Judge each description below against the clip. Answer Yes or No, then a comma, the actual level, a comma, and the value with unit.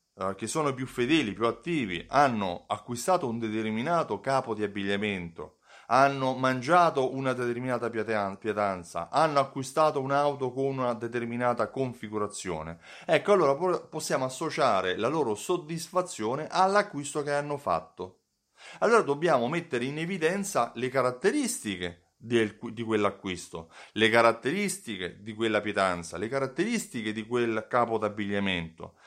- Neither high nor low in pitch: No, low, 120 Hz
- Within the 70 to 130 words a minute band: Yes, average, 120 wpm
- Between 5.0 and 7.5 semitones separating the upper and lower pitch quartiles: Yes, average, 5.3 semitones